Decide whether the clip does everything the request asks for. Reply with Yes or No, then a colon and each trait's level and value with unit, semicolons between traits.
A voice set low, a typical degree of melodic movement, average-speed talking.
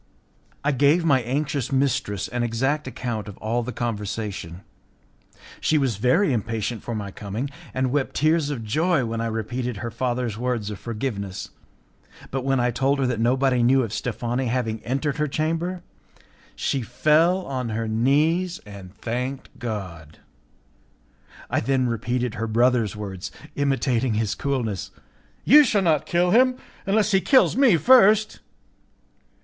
Yes: low, 125 Hz; average, 4.5 semitones; average, 150 wpm